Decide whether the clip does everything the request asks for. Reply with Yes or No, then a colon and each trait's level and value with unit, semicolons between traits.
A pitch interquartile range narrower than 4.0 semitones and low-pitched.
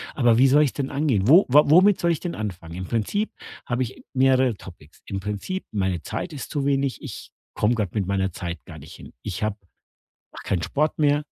No: wide, 7.1 semitones; low, 120 Hz